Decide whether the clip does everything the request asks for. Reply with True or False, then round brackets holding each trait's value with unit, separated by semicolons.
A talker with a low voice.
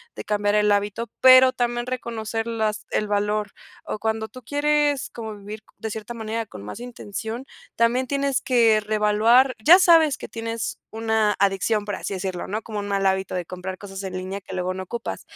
False (220 Hz)